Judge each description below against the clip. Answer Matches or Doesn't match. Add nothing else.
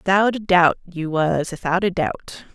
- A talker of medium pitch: Matches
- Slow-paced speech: Matches